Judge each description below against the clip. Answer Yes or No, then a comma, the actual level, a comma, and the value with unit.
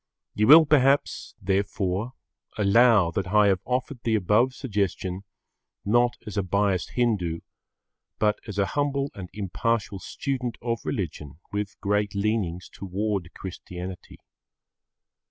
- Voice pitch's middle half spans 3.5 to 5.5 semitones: Yes, average, 3.9 semitones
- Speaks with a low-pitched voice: Yes, low, 105 Hz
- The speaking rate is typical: No, slow, 120 wpm